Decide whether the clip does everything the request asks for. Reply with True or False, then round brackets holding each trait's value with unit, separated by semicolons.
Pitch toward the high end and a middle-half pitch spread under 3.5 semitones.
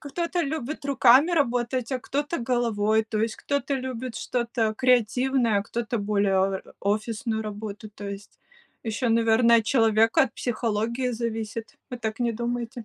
True (235 Hz; 2.6 semitones)